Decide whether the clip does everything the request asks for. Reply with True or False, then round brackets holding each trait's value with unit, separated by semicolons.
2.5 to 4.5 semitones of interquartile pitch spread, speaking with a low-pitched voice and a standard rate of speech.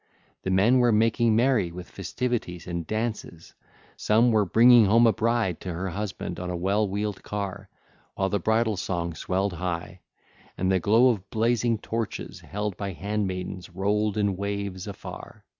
True (3.2 semitones; 100 Hz; 160 wpm)